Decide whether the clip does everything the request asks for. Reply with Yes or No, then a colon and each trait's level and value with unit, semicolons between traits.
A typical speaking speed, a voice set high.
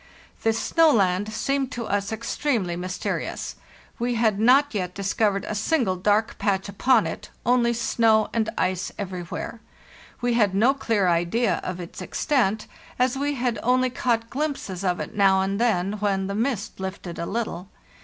Yes: average, 165 wpm; high, 215 Hz